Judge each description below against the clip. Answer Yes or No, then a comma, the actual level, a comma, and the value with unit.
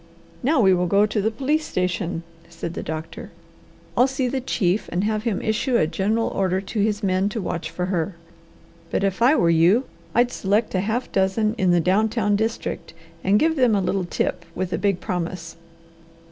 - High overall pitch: Yes, high, 200 Hz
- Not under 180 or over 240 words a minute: Yes, average, 200 wpm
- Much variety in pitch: No, average, 3.6 semitones